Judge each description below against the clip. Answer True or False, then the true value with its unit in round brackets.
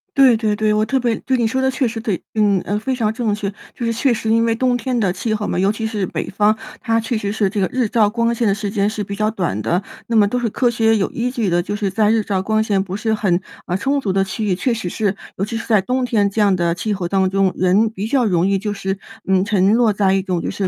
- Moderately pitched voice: False (215 Hz)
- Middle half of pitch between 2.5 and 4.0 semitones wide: True (2.8 semitones)